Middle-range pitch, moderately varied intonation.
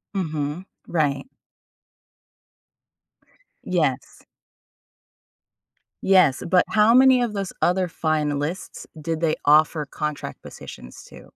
Yes: medium, 165 Hz; average, 4.2 semitones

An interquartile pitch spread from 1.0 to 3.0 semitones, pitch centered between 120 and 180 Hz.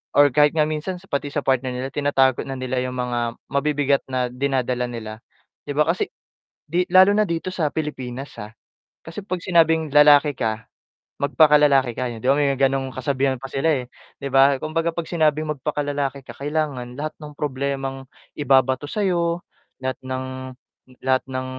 Yes: average, 2.7 semitones; medium, 140 Hz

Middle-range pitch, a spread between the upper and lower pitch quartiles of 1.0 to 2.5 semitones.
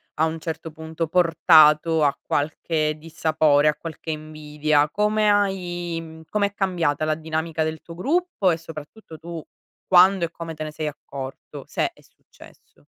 Yes: medium, 160 Hz; narrow, 2.1 semitones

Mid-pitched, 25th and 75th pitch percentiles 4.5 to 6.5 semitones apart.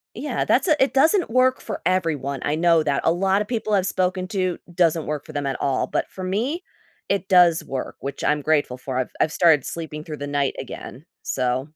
Yes: medium, 165 Hz; average, 5.0 semitones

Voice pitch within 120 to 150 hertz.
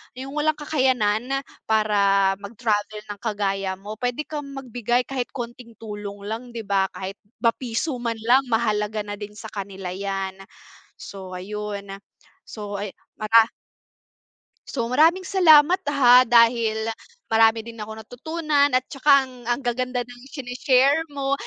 No: high, 230 Hz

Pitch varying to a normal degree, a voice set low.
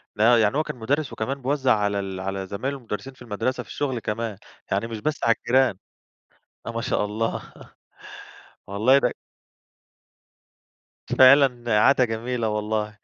Yes: average, 3.7 semitones; low, 115 Hz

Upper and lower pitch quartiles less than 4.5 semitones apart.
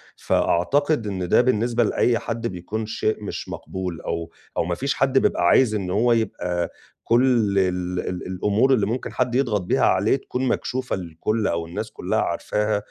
No: average, 5.0 semitones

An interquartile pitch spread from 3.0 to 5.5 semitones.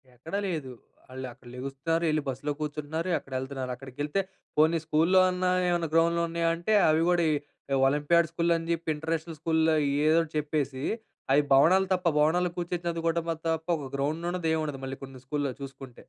Yes: average, 3.3 semitones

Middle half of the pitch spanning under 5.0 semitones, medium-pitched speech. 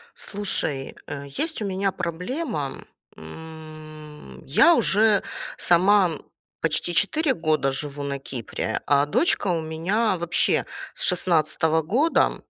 No: average, 5.3 semitones; medium, 160 Hz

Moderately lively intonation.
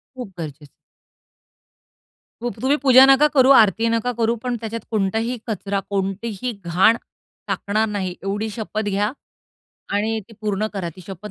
Yes: average, 3.0 semitones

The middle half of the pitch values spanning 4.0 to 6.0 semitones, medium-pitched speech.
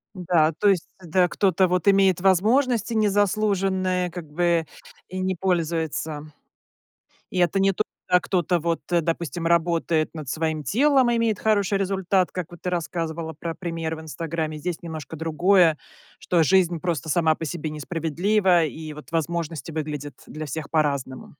No: average, 2.9 semitones; medium, 170 Hz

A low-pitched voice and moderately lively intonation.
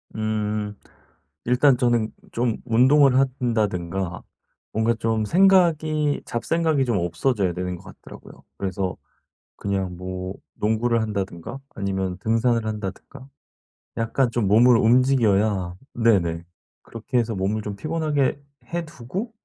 Yes: low, 115 Hz; average, 4.7 semitones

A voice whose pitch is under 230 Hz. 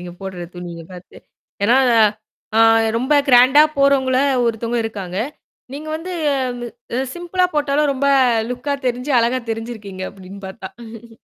No: high, 235 Hz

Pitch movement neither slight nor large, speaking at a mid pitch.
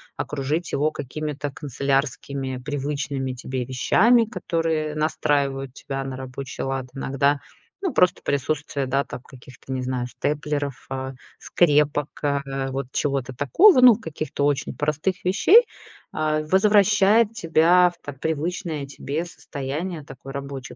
Yes: average, 3.2 semitones; medium, 145 Hz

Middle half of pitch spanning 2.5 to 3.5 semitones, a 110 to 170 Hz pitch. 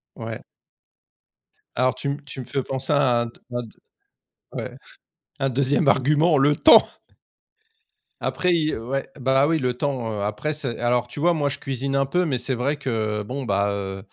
Yes: average, 3.0 semitones; low, 135 Hz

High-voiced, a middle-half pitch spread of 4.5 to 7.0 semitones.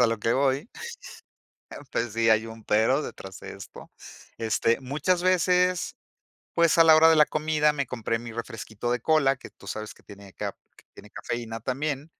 No: low, 130 Hz; wide, 5.4 semitones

